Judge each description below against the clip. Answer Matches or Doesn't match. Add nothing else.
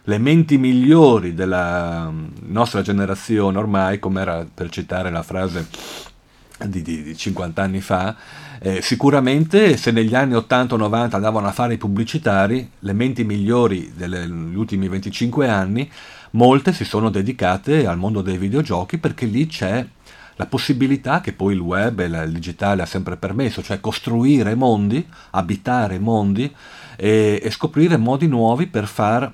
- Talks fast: Doesn't match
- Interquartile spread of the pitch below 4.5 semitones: Doesn't match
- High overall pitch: Doesn't match